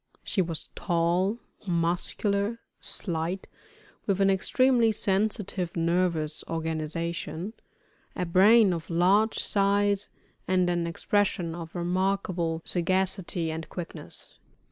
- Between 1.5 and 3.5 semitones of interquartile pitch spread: Yes, average, 2.9 semitones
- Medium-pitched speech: Yes, medium, 180 Hz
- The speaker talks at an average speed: No, slow, 100 wpm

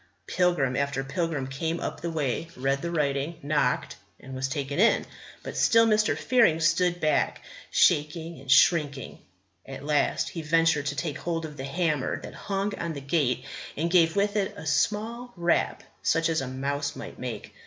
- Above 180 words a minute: No, average, 175 wpm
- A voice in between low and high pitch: Yes, medium, 155 Hz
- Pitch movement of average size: Yes, average, 3.7 semitones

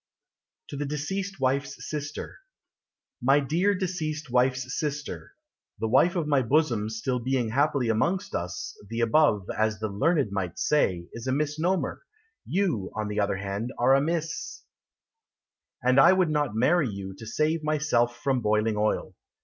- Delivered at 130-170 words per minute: Yes, average, 155 wpm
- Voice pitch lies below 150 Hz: Yes, low, 135 Hz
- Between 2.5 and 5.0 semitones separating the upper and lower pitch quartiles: No, wide, 5.6 semitones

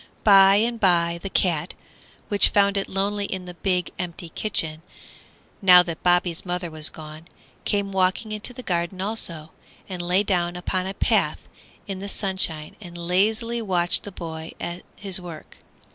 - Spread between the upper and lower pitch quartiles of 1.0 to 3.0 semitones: Yes, narrow, 2.5 semitones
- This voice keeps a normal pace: Yes, average, 160 wpm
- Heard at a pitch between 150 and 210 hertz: Yes, medium, 185 Hz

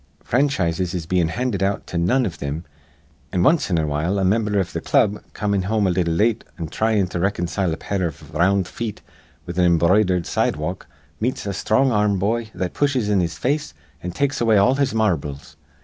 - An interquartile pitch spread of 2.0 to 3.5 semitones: No, average, 4.2 semitones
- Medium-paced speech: No, fast, 210 wpm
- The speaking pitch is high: No, very low, 95 Hz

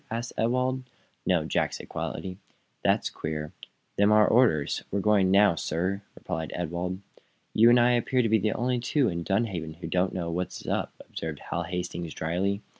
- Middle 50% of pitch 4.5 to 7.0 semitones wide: Yes, average, 4.9 semitones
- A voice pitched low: Yes, very low, 95 Hz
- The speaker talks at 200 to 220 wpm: No, average, 180 wpm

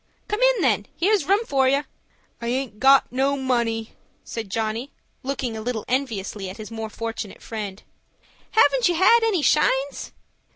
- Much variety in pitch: No, average, 4.6 semitones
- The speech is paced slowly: No, average, 160 wpm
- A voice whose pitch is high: Yes, very high, 255 Hz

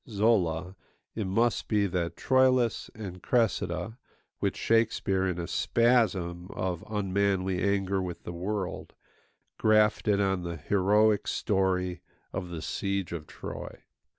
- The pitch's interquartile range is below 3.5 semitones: Yes, average, 3.1 semitones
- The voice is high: No, very low, 95 Hz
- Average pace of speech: No, slow, 125 wpm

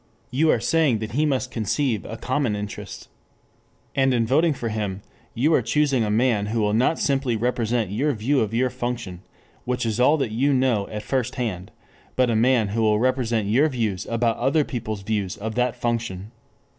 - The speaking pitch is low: Yes, low, 120 Hz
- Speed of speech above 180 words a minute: Yes, average, 195 wpm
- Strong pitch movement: No, average, 3.2 semitones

